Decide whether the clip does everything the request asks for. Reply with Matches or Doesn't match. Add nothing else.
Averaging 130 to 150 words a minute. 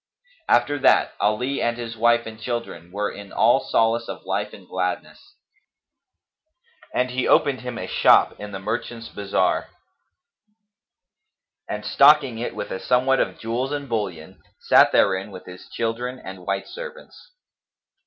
Matches